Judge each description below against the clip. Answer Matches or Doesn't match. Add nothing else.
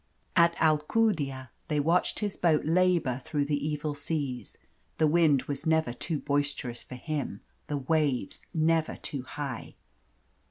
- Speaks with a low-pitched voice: Doesn't match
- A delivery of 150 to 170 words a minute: Doesn't match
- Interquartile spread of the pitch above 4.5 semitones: Doesn't match